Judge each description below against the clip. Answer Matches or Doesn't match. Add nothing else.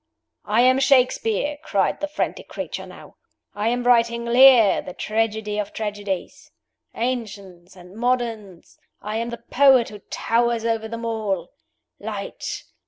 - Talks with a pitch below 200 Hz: Doesn't match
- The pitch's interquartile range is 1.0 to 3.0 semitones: Matches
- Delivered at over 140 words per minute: Doesn't match